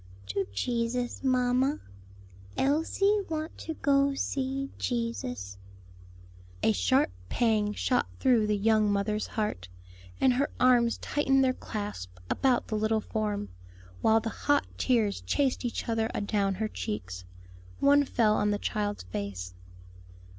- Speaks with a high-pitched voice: Yes, high, 225 Hz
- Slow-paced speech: Yes, slow, 130 wpm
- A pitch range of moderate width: Yes, average, 4.3 semitones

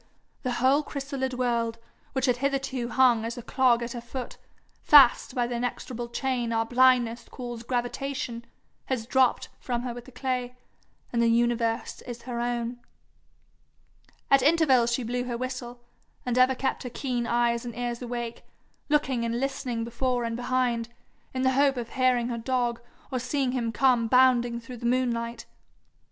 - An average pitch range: No, narrow, 1.6 semitones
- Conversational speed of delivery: Yes, average, 165 wpm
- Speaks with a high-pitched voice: Yes, high, 245 Hz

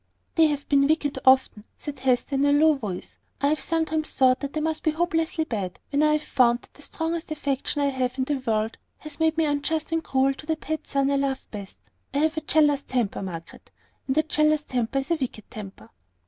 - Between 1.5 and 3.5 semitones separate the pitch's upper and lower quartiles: Yes, average, 3.2 semitones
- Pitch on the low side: No, very high, 285 Hz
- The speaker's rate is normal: No, fast, 220 wpm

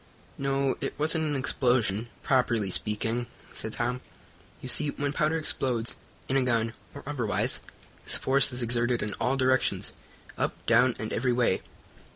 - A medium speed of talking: Yes, average, 155 wpm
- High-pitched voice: No, low, 125 Hz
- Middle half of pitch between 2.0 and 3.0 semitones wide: Yes, average, 2.7 semitones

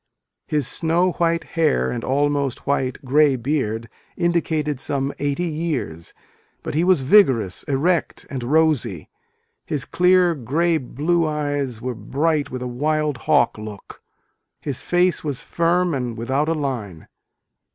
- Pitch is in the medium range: Yes, medium, 145 Hz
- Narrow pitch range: No, average, 4.4 semitones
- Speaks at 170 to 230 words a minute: No, average, 140 wpm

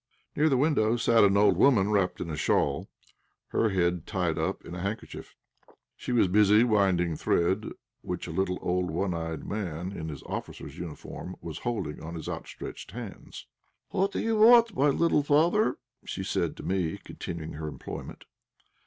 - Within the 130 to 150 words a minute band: No, average, 170 wpm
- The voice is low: Yes, very low, 95 Hz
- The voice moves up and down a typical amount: No, wide, 5.8 semitones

